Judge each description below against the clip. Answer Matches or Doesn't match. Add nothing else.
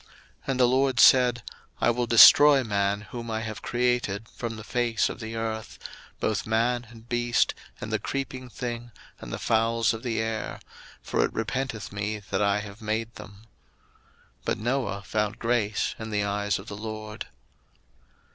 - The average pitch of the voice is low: Matches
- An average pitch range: Doesn't match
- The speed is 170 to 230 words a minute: Matches